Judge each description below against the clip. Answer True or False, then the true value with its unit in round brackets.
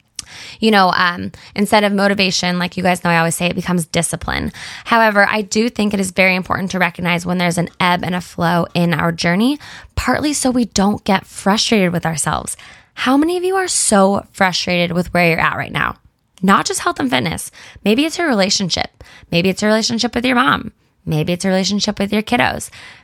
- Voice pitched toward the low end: False (190 Hz)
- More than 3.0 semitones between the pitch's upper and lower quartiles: True (3.7 semitones)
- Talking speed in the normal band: False (210 wpm)